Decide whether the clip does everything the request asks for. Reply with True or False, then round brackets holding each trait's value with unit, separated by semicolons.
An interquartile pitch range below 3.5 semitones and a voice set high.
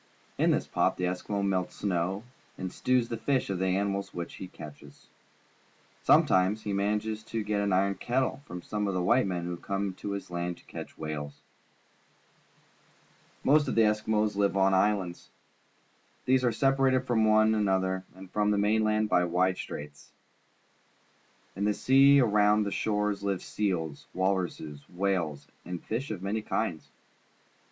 False (2.9 semitones; 100 Hz)